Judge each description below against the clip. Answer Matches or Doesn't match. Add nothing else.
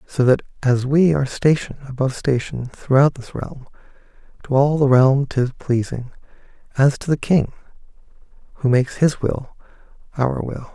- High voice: Doesn't match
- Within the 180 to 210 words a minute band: Doesn't match